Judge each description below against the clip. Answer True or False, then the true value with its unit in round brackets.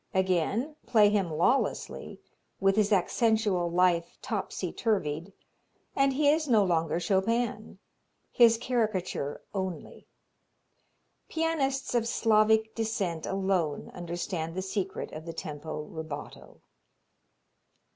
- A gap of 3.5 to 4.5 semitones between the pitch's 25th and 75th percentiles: False (4.9 semitones)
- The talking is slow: True (105 wpm)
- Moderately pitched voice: False (195 Hz)